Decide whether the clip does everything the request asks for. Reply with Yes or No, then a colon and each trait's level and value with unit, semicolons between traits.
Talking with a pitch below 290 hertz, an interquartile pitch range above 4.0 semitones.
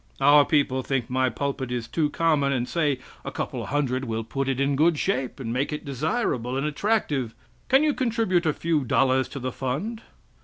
No: medium, 140 Hz; average, 3.5 semitones